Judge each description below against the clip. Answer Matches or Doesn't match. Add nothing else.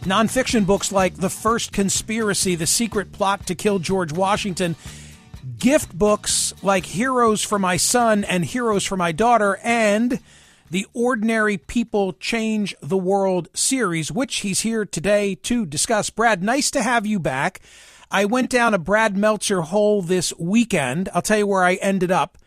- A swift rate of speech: Doesn't match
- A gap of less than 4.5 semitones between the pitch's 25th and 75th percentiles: Matches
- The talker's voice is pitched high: Matches